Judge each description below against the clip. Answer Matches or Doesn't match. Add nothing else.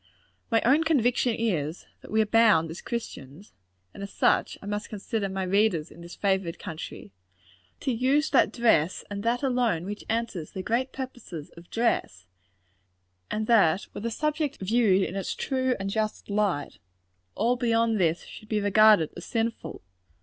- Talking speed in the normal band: Matches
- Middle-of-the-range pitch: Doesn't match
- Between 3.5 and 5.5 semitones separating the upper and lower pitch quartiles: Matches